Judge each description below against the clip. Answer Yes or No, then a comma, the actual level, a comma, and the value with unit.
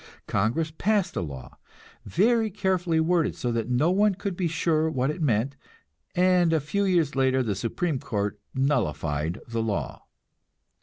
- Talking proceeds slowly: No, average, 155 wpm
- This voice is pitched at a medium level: Yes, medium, 155 Hz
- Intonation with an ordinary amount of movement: No, wide, 7.6 semitones